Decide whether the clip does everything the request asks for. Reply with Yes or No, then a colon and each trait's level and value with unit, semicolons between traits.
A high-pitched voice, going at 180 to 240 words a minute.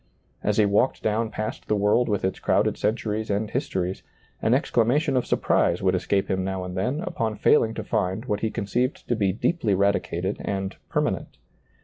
No: low, 105 Hz; average, 185 wpm